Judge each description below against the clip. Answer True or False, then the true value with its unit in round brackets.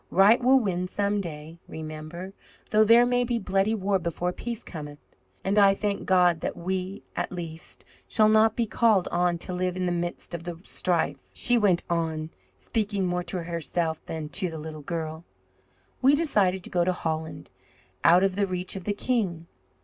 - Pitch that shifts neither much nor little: True (3.5 semitones)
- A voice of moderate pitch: True (180 Hz)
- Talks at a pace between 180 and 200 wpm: True (185 wpm)